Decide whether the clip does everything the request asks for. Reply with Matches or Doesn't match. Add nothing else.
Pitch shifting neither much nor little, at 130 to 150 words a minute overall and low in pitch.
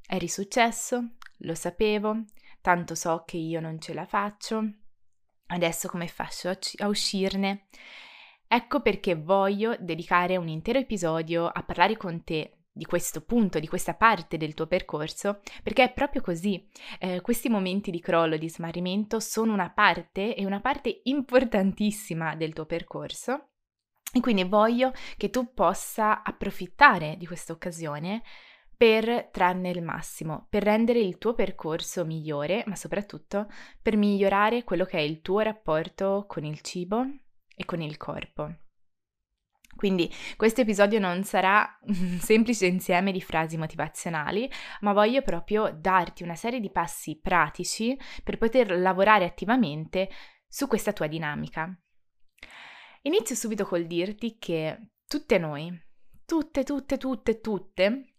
Doesn't match